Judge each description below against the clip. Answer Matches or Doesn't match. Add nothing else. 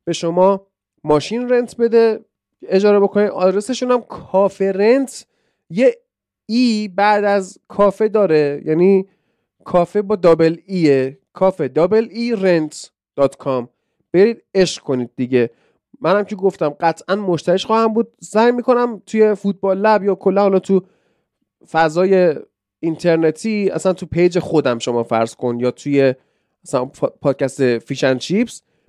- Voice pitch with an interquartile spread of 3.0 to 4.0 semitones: Doesn't match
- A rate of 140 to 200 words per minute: Doesn't match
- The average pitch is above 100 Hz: Matches